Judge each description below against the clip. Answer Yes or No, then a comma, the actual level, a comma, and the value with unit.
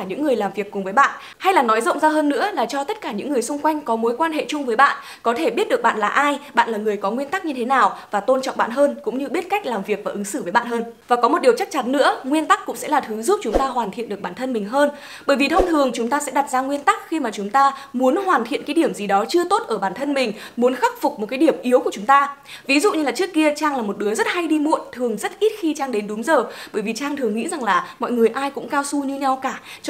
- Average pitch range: Yes, average, 5.0 semitones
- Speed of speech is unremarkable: No, fast, 325 wpm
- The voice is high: Yes, very high, 275 Hz